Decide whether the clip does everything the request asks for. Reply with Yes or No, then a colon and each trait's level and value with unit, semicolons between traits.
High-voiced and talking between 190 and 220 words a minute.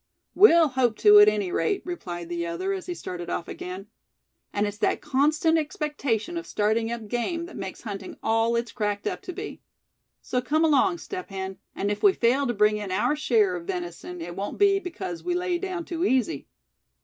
Yes: high, 240 Hz; average, 200 wpm